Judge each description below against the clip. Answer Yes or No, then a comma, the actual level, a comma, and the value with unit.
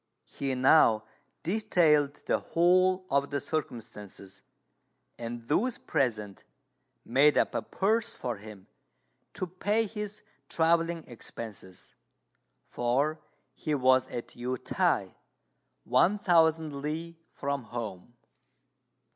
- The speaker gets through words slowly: Yes, slow, 105 wpm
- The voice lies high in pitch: No, medium, 145 Hz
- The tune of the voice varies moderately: No, wide, 6.0 semitones